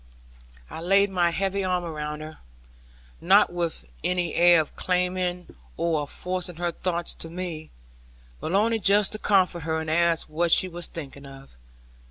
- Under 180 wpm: Yes, average, 165 wpm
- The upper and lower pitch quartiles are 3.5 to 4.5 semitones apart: No, narrow, 2.4 semitones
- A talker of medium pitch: Yes, medium, 175 Hz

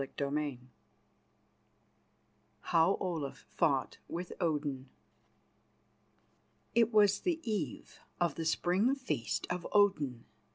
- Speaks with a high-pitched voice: No, medium, 170 Hz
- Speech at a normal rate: No, slow, 95 wpm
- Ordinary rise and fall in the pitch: No, wide, 5.9 semitones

